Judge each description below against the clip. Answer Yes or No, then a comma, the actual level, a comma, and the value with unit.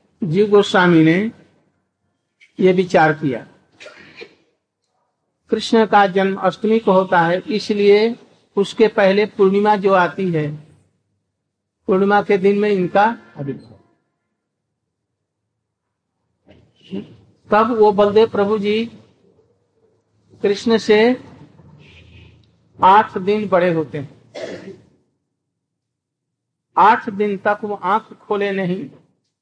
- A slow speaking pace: Yes, slow, 90 wpm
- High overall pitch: Yes, high, 200 Hz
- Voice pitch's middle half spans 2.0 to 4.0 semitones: Yes, average, 3.3 semitones